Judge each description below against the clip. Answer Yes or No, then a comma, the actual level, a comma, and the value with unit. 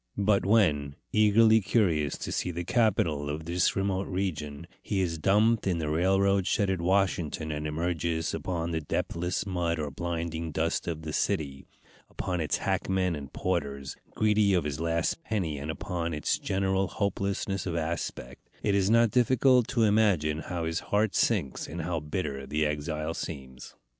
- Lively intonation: No, average, 4.2 semitones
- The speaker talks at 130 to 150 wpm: No, average, 165 wpm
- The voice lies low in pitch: Yes, very low, 85 Hz